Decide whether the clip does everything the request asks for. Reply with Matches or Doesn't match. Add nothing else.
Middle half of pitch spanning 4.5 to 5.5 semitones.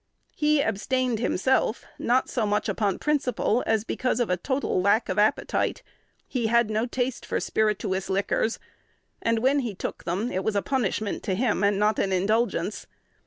Doesn't match